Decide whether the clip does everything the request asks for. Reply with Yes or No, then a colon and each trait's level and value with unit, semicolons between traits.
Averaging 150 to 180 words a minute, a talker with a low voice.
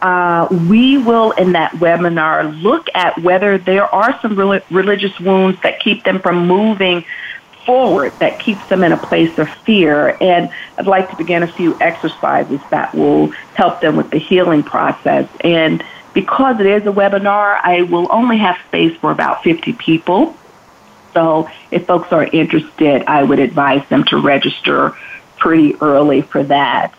No: average, 165 wpm; medium, 185 Hz